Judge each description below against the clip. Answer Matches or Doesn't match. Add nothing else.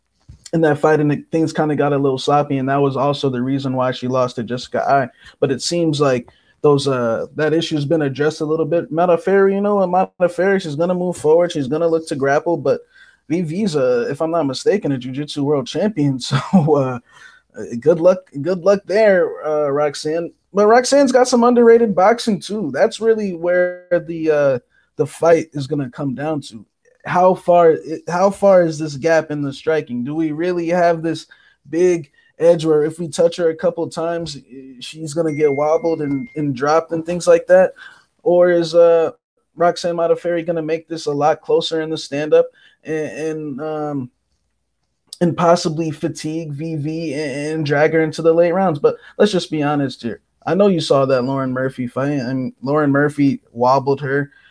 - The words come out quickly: Doesn't match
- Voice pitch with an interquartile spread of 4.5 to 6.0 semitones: Doesn't match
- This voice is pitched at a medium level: Matches